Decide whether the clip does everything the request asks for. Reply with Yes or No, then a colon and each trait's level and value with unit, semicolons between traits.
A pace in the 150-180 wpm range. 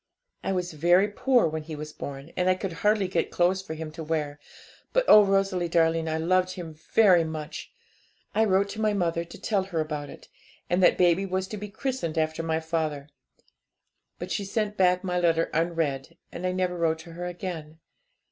No: fast, 205 wpm